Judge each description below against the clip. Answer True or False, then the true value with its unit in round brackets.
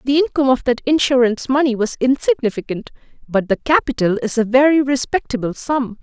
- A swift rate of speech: False (160 wpm)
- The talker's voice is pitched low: False (250 Hz)